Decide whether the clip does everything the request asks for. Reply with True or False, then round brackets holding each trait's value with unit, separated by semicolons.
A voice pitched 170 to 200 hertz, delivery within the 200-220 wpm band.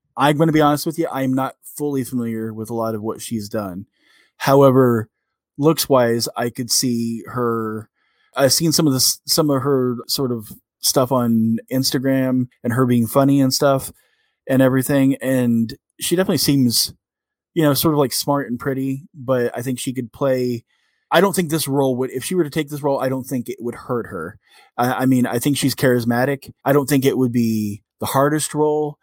False (130 Hz; 205 wpm)